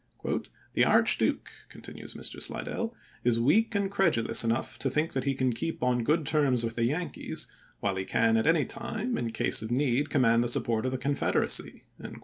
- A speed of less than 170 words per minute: No, average, 190 wpm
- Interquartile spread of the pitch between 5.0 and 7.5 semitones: Yes, wide, 5.5 semitones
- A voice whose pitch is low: Yes, low, 130 Hz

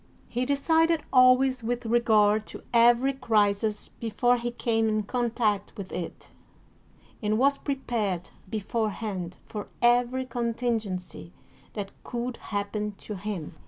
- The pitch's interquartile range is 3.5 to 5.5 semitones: No, average, 2.9 semitones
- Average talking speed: No, slow, 120 wpm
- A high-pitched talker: Yes, high, 230 Hz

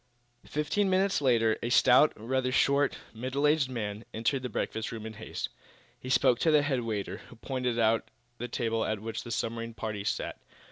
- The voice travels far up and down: No, average, 3.4 semitones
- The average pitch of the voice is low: Yes, low, 120 Hz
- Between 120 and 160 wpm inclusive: No, average, 185 wpm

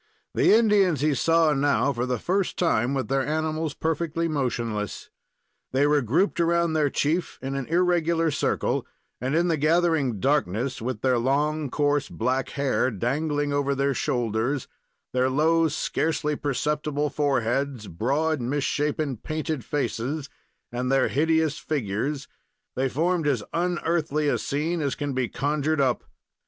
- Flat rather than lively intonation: No, average, 3.2 semitones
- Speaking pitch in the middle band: Yes, medium, 145 Hz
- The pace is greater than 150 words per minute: No, average, 145 wpm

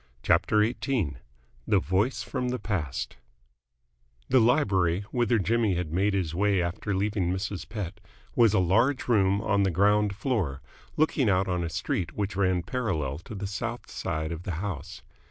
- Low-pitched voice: Yes, low, 100 Hz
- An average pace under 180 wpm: Yes, average, 165 wpm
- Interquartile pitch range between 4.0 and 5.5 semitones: No, average, 3.6 semitones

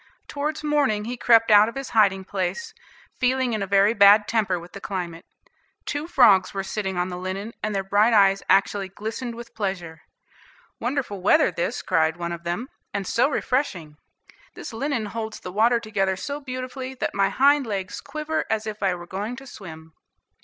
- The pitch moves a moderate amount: Yes, average, 4.6 semitones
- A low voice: No, high, 210 Hz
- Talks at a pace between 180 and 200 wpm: Yes, average, 185 wpm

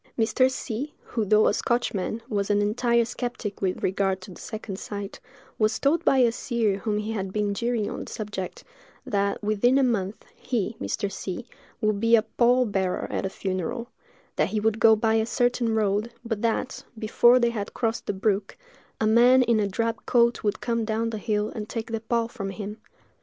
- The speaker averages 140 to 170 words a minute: No, average, 200 wpm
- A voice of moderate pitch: No, high, 220 Hz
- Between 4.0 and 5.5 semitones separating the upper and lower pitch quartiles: No, narrow, 2.5 semitones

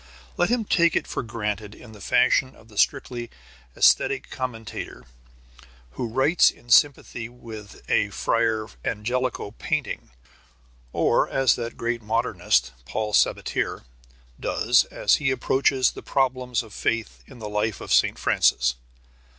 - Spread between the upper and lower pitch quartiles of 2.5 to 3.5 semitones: Yes, average, 3.1 semitones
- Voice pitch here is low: Yes, low, 115 Hz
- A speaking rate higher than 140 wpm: No, slow, 135 wpm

